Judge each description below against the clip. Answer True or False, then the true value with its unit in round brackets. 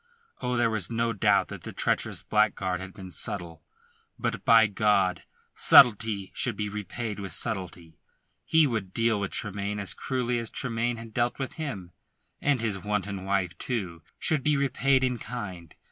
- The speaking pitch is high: False (105 Hz)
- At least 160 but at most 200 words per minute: True (165 wpm)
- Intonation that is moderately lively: True (3.8 semitones)